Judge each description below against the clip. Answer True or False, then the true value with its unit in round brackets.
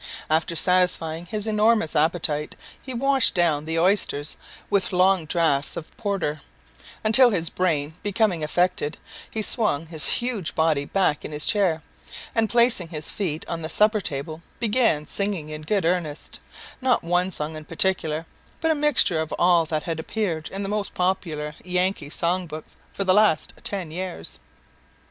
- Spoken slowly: False (160 wpm)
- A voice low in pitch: False (175 Hz)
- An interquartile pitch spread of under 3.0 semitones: False (4.5 semitones)